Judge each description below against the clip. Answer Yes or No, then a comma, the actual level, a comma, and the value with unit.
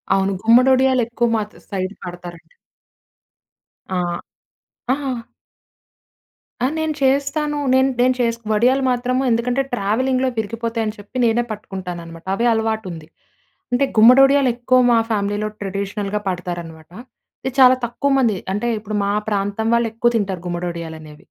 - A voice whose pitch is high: Yes, high, 220 Hz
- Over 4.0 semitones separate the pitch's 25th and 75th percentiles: Yes, average, 4.5 semitones